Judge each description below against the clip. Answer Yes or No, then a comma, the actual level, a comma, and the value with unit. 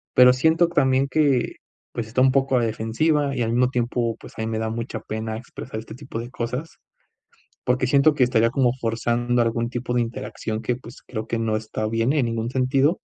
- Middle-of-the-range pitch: No, low, 120 Hz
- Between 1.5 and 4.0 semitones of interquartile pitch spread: Yes, narrow, 2.5 semitones